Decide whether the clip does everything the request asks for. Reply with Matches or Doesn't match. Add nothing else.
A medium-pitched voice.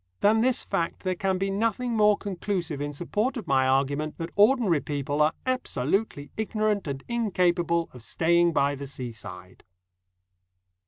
Matches